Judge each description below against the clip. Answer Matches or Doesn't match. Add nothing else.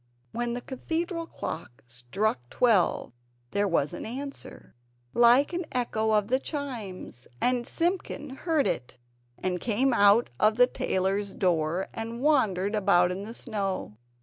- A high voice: Matches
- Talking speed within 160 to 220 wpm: Doesn't match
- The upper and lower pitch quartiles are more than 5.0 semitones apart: Matches